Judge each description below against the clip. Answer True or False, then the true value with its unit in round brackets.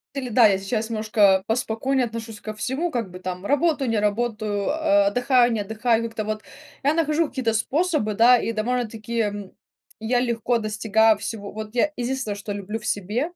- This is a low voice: False (225 Hz)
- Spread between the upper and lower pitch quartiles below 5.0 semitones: True (2.9 semitones)